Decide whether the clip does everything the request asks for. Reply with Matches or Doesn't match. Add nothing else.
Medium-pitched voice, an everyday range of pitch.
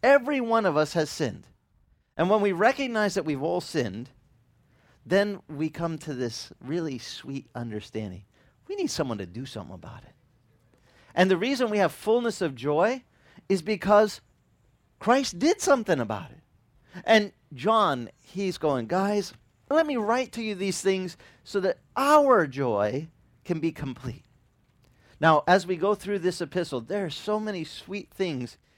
Doesn't match